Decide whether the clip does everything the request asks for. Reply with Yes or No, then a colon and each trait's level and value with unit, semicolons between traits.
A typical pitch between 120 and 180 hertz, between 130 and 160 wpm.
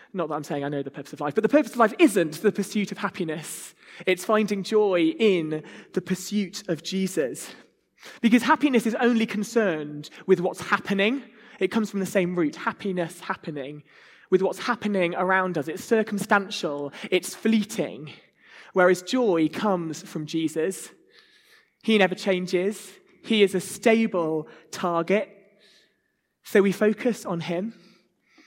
No: high, 195 Hz; average, 150 wpm